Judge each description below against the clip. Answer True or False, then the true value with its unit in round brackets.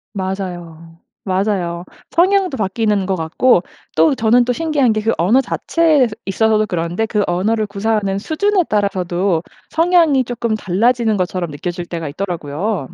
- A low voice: False (205 Hz)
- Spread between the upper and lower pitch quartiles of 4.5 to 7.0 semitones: True (5.1 semitones)